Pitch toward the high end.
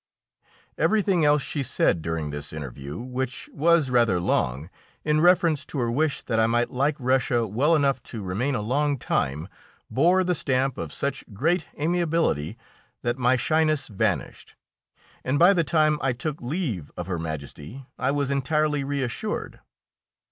No: low, 135 Hz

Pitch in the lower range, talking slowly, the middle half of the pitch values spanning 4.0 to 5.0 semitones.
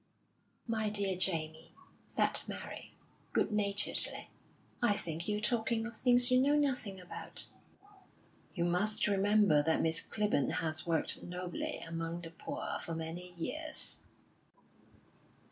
No: high, 195 Hz; slow, 125 wpm; average, 4.7 semitones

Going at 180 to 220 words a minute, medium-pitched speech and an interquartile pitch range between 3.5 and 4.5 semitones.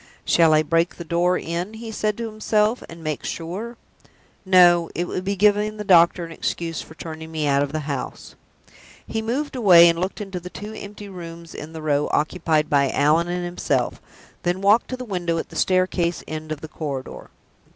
Yes: average, 200 wpm; medium, 175 Hz; average, 4.1 semitones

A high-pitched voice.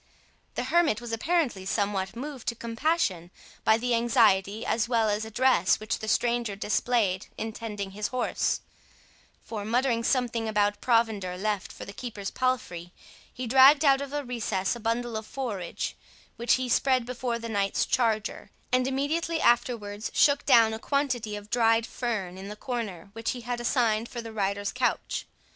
Yes: high, 230 Hz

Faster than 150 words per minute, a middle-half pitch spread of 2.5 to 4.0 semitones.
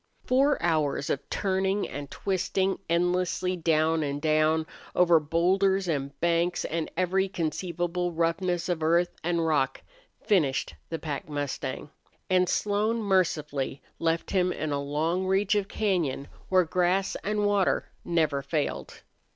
No: slow, 135 wpm; average, 3.3 semitones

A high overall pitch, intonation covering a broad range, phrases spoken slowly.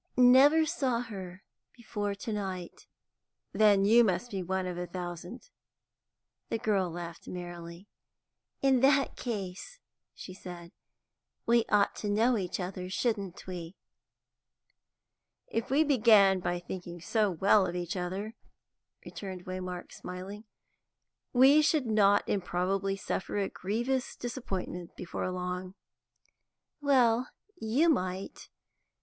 No: high, 195 Hz; average, 4.4 semitones; slow, 120 wpm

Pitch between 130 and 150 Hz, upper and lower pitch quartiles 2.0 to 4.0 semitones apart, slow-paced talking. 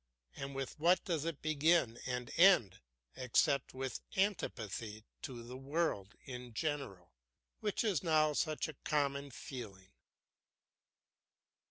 No: medium, 140 Hz; average, 4.7 semitones; slow, 120 wpm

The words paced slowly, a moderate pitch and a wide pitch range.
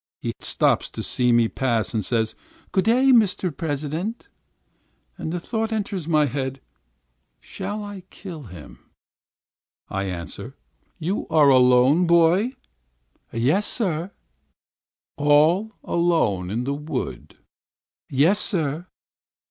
Yes: slow, 115 wpm; medium, 155 Hz; wide, 7.1 semitones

